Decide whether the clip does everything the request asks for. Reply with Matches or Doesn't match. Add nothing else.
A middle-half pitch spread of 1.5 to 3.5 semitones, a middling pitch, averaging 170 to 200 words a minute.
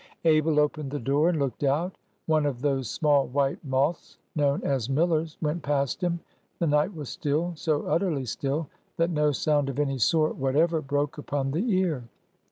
Matches